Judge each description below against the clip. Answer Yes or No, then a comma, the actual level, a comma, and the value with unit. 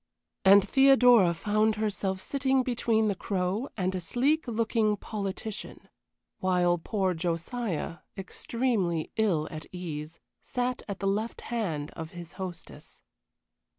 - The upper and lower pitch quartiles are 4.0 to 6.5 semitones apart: Yes, average, 4.5 semitones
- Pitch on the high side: Yes, high, 200 Hz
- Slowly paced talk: Yes, slow, 120 wpm